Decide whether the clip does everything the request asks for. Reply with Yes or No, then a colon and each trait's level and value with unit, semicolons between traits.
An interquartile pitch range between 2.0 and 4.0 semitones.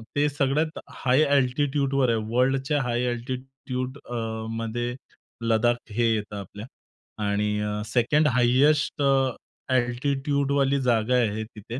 Yes: average, 2.9 semitones